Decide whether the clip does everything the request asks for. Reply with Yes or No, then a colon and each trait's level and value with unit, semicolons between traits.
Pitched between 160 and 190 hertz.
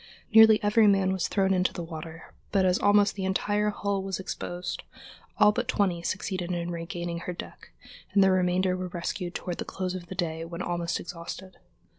Yes: medium, 185 Hz